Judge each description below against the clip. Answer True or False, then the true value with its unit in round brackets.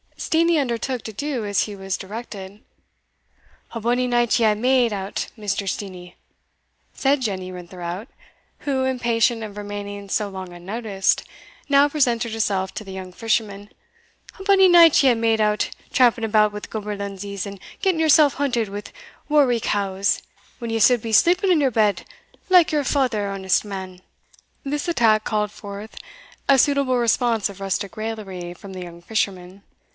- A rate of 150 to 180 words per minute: True (155 wpm)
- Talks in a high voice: True (215 Hz)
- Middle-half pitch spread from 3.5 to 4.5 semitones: True (4.1 semitones)